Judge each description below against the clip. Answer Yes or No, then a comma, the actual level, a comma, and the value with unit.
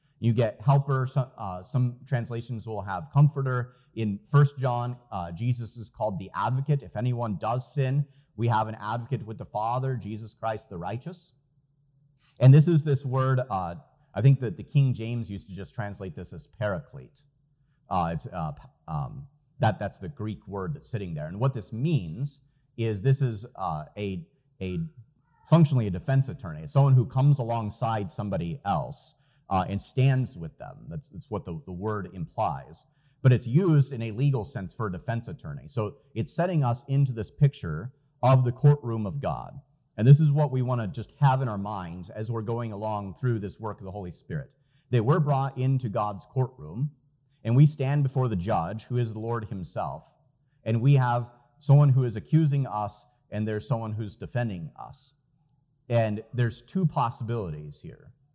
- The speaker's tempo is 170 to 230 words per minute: Yes, average, 185 wpm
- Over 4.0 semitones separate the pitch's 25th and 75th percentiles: Yes, average, 4.4 semitones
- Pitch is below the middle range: Yes, low, 125 Hz